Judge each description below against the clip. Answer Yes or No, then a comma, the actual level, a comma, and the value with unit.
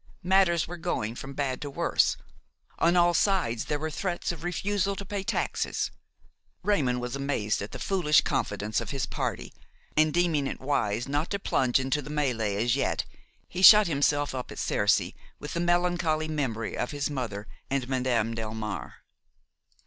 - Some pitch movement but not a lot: No, wide, 6.0 semitones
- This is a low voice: No, medium, 145 Hz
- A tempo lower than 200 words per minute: Yes, average, 170 wpm